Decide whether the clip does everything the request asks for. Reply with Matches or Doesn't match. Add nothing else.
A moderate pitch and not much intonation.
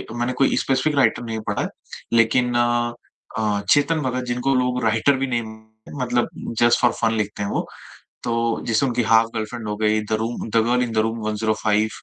Doesn't match